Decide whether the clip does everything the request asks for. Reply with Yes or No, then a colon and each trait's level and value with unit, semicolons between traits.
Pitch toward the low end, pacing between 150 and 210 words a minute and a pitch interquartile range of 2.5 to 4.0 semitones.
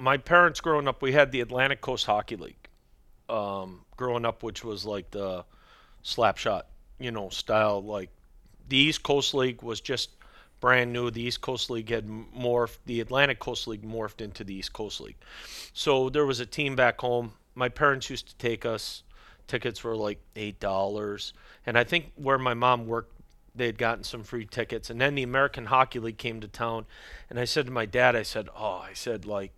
Yes: low, 120 Hz; average, 200 wpm; average, 3.2 semitones